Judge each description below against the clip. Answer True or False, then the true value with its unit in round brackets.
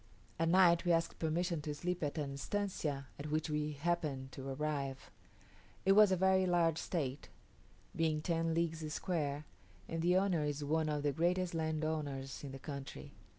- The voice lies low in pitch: False (155 Hz)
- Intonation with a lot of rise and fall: False (2.9 semitones)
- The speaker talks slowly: False (170 wpm)